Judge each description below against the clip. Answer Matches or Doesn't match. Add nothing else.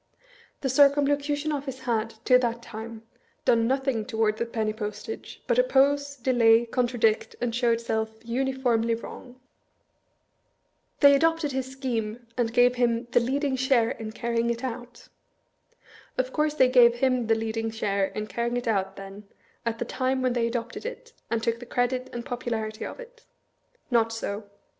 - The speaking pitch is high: Matches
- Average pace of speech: Matches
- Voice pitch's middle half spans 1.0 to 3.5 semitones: Matches